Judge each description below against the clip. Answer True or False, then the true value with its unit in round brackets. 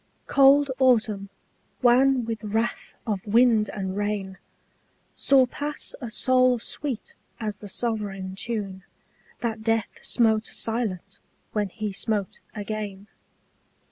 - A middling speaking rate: False (110 wpm)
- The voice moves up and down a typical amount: True (3.1 semitones)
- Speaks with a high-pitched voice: True (220 Hz)